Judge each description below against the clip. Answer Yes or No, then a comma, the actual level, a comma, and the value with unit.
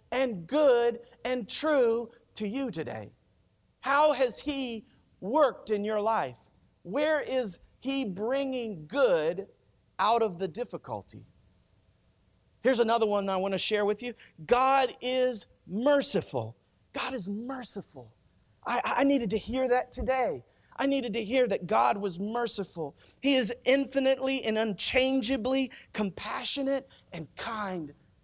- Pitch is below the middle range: No, high, 230 Hz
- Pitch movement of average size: No, wide, 6.2 semitones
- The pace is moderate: No, slow, 130 wpm